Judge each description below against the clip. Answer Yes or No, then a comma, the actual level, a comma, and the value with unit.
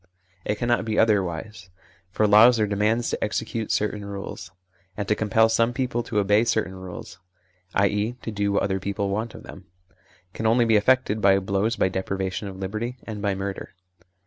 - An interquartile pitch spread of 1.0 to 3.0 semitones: Yes, narrow, 2.4 semitones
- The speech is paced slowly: No, average, 180 wpm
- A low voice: Yes, low, 105 Hz